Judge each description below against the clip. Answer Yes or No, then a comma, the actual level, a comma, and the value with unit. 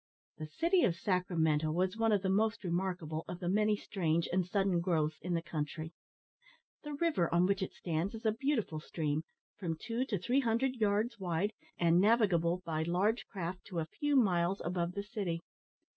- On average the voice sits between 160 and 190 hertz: Yes, medium, 185 Hz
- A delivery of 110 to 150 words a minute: No, average, 185 wpm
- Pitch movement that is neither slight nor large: Yes, average, 4.3 semitones